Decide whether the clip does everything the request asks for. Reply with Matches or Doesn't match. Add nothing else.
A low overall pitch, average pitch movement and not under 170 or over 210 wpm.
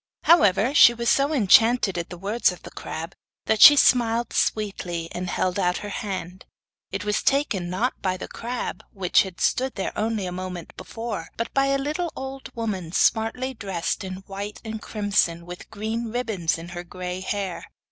Doesn't match